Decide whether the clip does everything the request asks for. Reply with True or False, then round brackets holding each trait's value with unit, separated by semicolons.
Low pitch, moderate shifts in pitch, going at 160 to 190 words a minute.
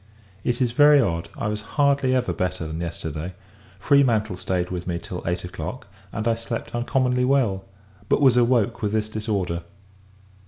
False (110 Hz; 5.7 semitones; 165 wpm)